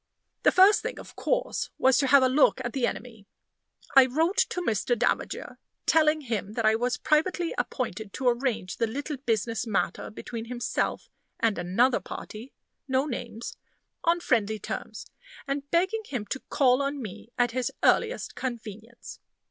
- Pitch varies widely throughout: No, average, 4.0 semitones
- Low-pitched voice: No, very high, 250 Hz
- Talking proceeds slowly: No, average, 160 wpm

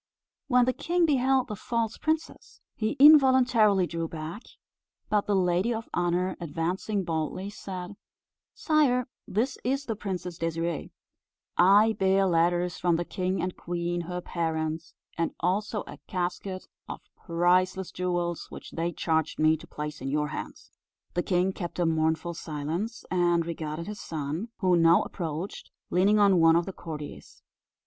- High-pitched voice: No, medium, 180 Hz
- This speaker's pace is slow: No, average, 150 wpm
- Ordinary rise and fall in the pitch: Yes, average, 3.9 semitones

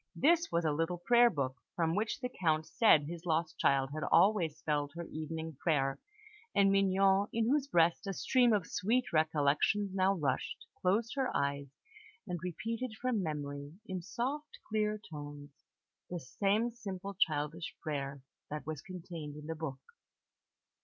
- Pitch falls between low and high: Yes, medium, 170 Hz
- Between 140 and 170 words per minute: Yes, average, 155 wpm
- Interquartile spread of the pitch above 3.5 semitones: Yes, wide, 5.5 semitones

